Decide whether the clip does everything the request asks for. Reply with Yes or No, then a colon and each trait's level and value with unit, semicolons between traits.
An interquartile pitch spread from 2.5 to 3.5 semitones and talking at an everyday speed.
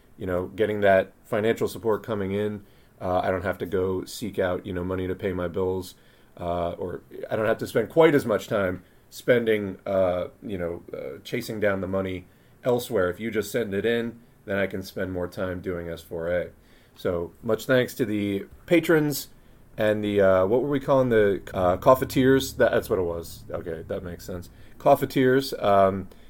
No: average, 4.5 semitones; average, 195 wpm